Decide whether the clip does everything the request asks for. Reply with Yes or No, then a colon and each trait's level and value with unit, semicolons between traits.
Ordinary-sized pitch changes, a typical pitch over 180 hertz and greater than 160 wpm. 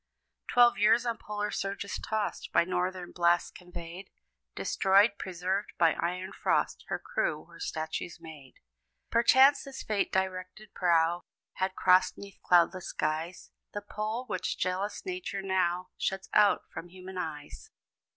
No: average, 3.1 semitones; high, 190 Hz; slow, 135 wpm